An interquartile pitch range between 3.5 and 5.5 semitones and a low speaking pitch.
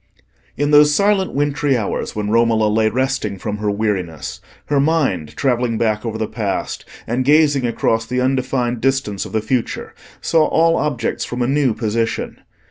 Yes: average, 4.4 semitones; low, 120 Hz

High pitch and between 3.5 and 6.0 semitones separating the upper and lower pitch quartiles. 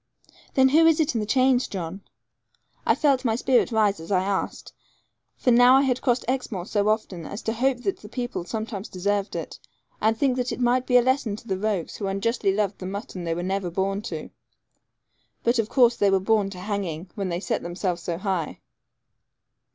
Yes: high, 210 Hz; average, 4.4 semitones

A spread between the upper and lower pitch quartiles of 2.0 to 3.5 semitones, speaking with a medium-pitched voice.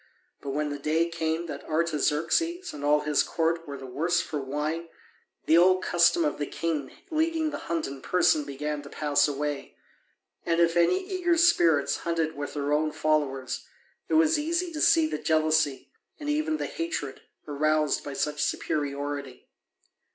No: average, 3.9 semitones; medium, 155 Hz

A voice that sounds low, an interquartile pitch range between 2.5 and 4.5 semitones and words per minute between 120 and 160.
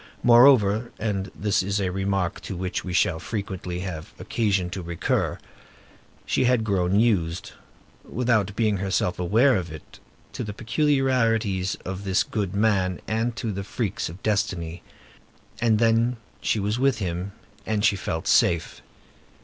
Yes: low, 100 Hz; average, 3.5 semitones; average, 140 wpm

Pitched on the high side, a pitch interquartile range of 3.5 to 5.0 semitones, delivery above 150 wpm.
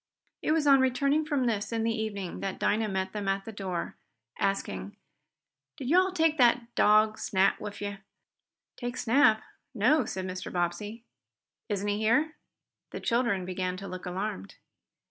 Yes: high, 215 Hz; average, 4.3 semitones; average, 165 wpm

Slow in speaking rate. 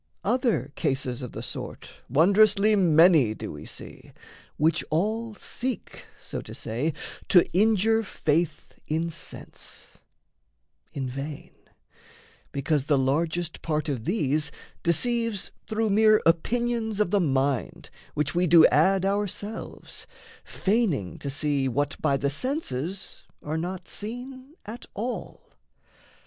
Yes: slow, 120 wpm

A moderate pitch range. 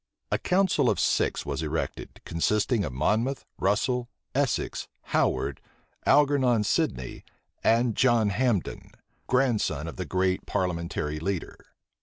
No: wide, 6.9 semitones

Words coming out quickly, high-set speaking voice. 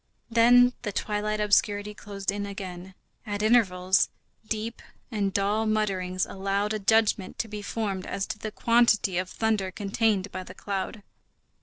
No: average, 150 wpm; high, 205 Hz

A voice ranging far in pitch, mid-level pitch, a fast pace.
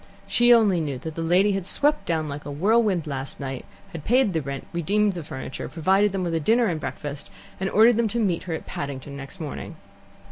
Yes: wide, 6.0 semitones; medium, 170 Hz; fast, 220 wpm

